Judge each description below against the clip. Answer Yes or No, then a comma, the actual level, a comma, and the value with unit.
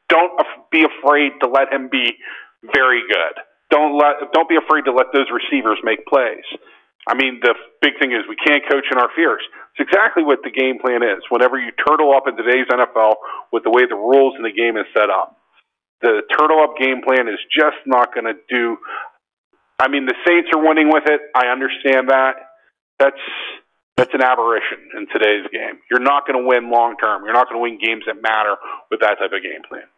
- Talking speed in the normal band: No, fast, 215 wpm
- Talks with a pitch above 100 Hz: Yes, low, 135 Hz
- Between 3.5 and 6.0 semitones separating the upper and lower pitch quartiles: No, average, 3.0 semitones